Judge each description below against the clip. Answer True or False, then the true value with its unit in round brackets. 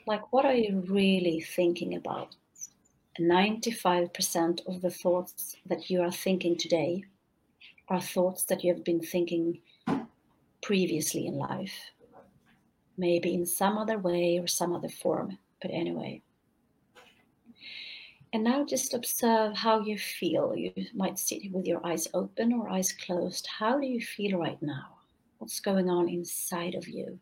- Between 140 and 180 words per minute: True (150 wpm)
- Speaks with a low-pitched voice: False (180 Hz)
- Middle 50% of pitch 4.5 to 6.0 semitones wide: False (3.6 semitones)